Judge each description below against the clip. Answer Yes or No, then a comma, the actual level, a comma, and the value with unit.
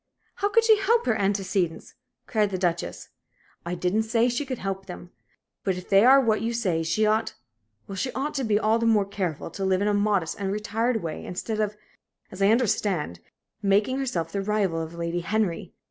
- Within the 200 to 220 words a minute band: Yes, fast, 205 wpm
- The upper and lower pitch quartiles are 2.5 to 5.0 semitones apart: Yes, average, 3.8 semitones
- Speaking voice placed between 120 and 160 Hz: No, high, 205 Hz